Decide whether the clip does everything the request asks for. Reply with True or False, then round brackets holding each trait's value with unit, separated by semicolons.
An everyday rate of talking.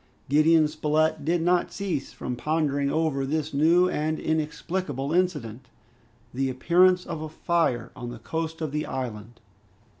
True (145 wpm)